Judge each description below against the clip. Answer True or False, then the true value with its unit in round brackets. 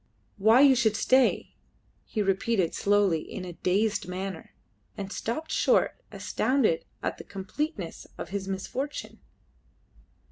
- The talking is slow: True (120 wpm)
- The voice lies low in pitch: False (205 Hz)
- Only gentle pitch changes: False (5.0 semitones)